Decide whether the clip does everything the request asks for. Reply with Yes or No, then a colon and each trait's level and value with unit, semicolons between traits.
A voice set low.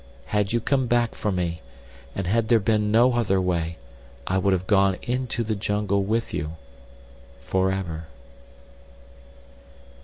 Yes: very low, 95 Hz